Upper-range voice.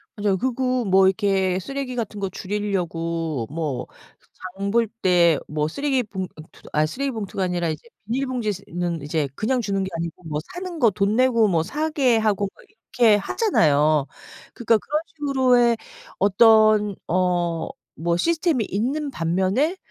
Yes: high, 205 Hz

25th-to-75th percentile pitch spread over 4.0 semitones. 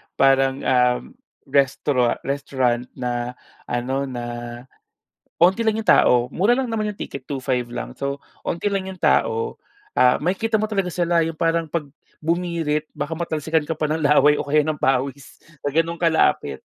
Yes: average, 4.6 semitones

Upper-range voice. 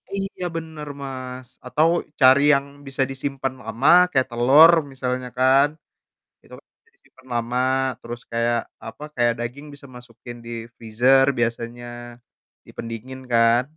No: low, 130 Hz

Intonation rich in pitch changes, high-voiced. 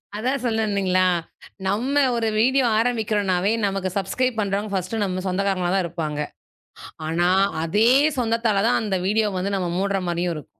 No: average, 3.3 semitones; high, 200 Hz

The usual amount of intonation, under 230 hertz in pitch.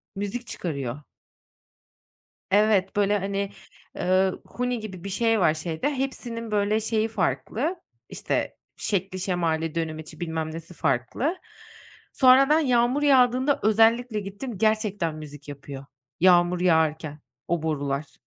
No: wide, 6.1 semitones; high, 195 Hz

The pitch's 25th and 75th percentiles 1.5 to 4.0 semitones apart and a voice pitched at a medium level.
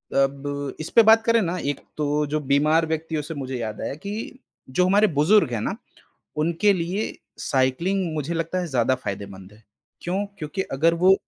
No: average, 5.1 semitones; medium, 155 Hz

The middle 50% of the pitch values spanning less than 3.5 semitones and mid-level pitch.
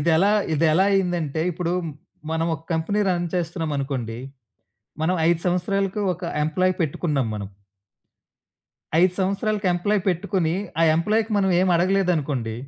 Yes: average, 3.0 semitones; medium, 175 Hz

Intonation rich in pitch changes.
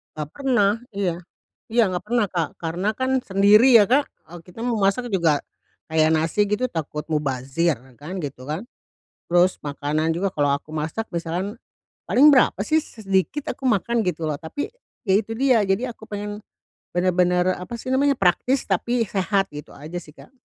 Yes: wide, 6.1 semitones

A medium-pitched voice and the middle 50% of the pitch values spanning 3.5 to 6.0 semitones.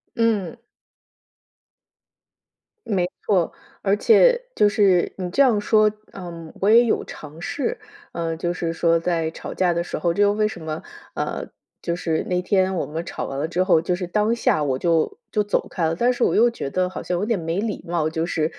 Yes: medium, 180 Hz; average, 4.0 semitones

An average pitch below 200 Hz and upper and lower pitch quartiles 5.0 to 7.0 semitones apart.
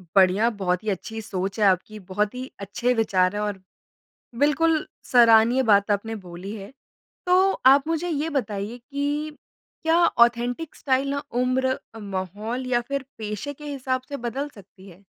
No: high, 235 Hz; wide, 5.5 semitones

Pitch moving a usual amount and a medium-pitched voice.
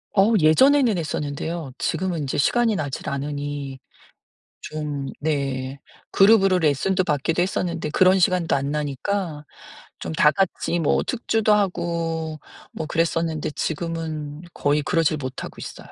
Yes: average, 4.0 semitones; medium, 160 Hz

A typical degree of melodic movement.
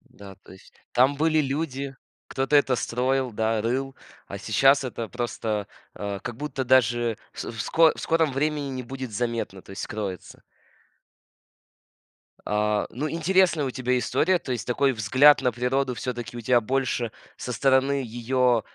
Yes: average, 3.0 semitones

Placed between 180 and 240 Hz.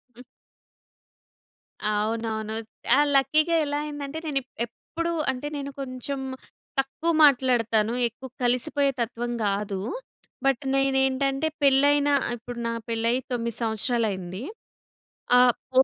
No: very high, 255 Hz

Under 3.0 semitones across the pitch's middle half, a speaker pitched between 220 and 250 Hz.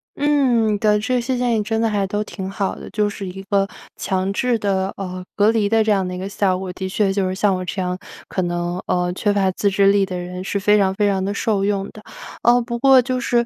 No: narrow, 2.5 semitones; high, 200 Hz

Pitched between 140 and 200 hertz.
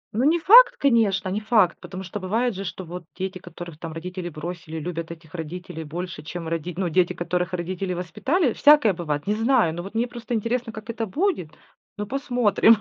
Yes: medium, 185 Hz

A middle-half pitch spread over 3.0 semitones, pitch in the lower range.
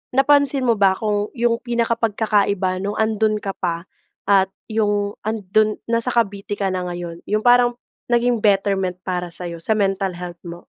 No: average, 3.4 semitones; high, 205 Hz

